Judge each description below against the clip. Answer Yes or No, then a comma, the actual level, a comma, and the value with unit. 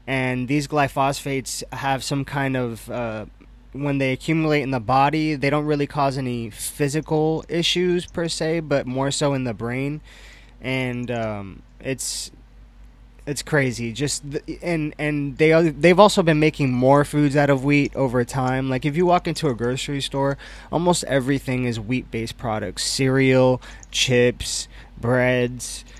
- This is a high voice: No, low, 135 Hz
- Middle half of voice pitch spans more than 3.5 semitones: No, average, 3.1 semitones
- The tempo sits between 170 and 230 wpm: No, average, 155 wpm